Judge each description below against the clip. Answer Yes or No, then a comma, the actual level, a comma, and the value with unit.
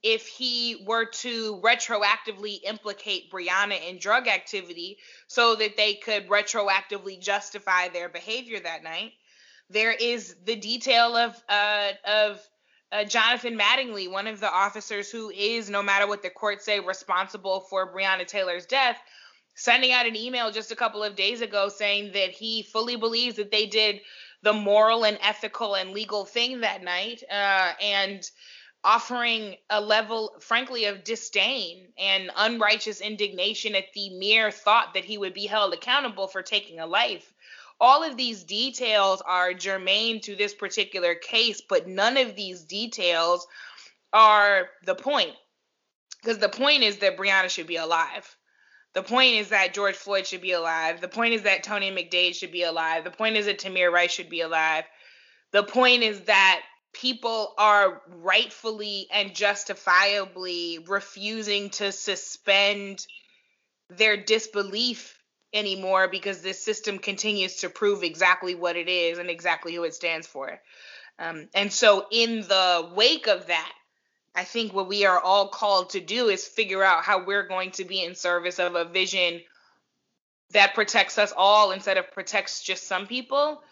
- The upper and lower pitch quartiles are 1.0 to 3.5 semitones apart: Yes, average, 2.8 semitones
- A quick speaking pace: No, average, 160 wpm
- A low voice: No, high, 205 Hz